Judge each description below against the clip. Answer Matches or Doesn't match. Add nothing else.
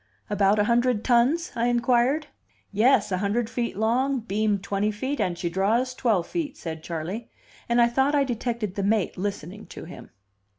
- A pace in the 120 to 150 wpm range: Doesn't match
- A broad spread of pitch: Doesn't match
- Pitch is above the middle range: Matches